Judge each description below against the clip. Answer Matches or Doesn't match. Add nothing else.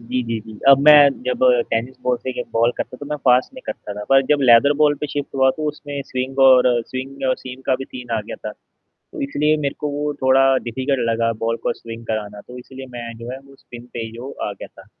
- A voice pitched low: Matches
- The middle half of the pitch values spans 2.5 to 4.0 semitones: Matches